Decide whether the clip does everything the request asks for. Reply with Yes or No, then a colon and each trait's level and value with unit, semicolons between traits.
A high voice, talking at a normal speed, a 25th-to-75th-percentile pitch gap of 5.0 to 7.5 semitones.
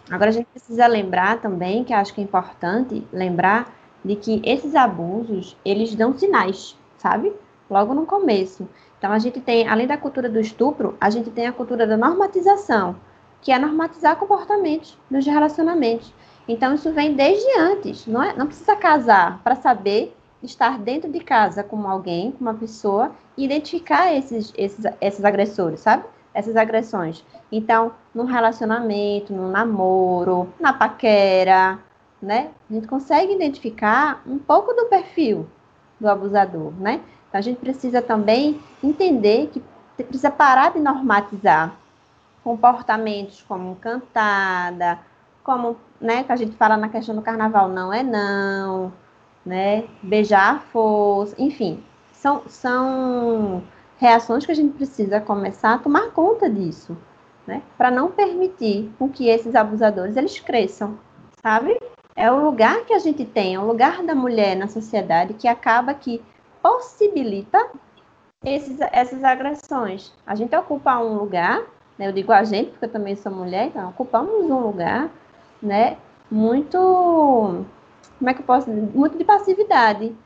Yes: high, 230 Hz; average, 150 wpm; wide, 5.5 semitones